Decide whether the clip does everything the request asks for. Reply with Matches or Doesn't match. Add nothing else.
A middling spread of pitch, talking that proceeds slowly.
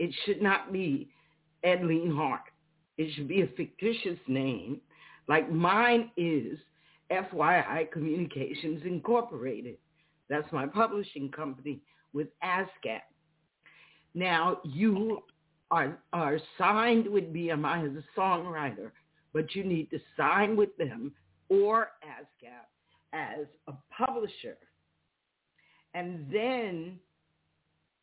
Matches